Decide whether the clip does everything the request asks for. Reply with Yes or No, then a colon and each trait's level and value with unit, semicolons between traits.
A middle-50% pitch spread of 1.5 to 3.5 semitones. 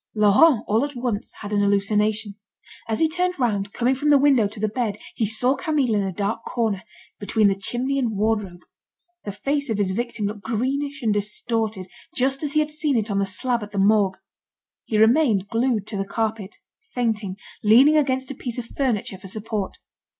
No: average, 4.2 semitones